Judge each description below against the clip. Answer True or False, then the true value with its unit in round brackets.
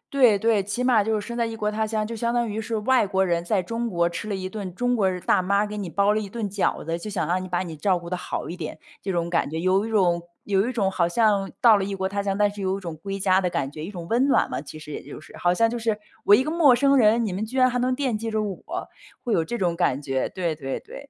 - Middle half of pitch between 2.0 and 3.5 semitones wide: False (4.1 semitones)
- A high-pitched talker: True (200 Hz)